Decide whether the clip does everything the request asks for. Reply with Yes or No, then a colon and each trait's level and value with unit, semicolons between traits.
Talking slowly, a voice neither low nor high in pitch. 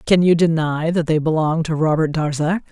No: average, 200 wpm; medium, 160 Hz